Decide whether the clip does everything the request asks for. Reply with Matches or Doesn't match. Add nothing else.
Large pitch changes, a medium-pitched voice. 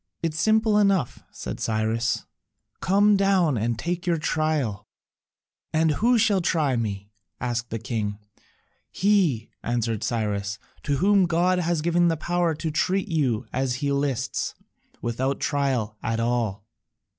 Matches